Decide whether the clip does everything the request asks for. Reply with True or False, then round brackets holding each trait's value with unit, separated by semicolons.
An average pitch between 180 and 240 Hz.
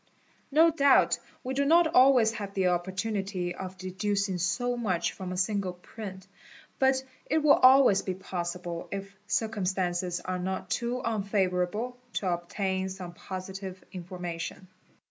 True (190 Hz)